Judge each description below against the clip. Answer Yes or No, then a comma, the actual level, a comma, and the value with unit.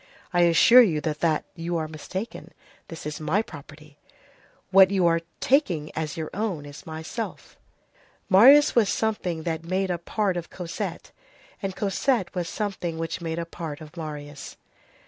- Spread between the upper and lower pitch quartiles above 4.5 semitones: No, average, 3.7 semitones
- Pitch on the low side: No, medium, 170 Hz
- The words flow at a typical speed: Yes, average, 150 wpm